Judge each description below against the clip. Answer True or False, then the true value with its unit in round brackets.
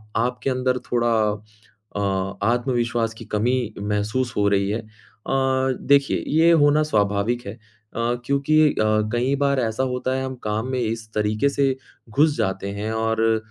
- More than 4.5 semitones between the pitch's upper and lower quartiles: False (3.7 semitones)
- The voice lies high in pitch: False (120 Hz)